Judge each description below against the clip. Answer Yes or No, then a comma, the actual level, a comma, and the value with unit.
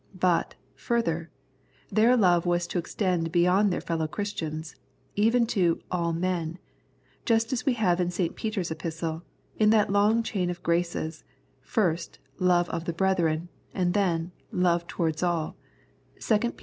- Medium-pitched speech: Yes, medium, 175 Hz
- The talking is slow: No, average, 155 wpm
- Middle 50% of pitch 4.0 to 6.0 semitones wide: No, average, 3.5 semitones